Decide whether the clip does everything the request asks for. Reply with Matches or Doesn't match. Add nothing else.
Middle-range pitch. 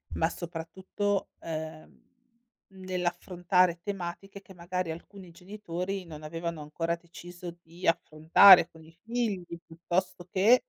Matches